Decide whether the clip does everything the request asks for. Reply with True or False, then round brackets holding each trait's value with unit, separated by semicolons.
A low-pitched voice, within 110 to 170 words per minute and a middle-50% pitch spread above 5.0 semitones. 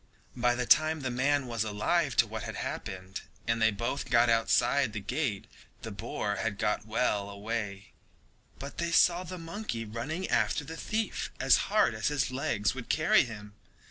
False (120 Hz; 180 wpm; 5.5 semitones)